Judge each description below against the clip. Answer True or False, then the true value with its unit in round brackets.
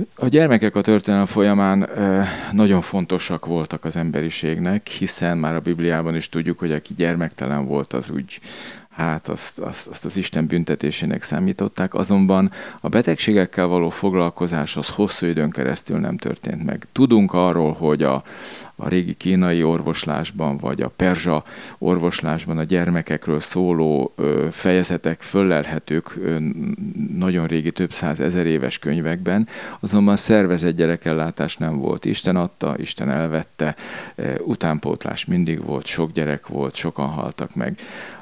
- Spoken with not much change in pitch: False (3.2 semitones)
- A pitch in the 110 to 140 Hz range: False (85 Hz)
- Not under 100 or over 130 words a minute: False (140 wpm)